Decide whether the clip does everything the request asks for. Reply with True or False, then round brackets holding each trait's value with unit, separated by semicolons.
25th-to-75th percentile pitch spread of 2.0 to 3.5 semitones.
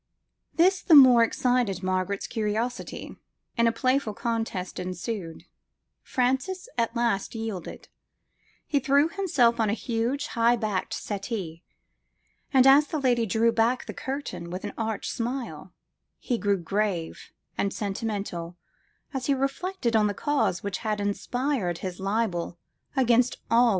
False (4.5 semitones)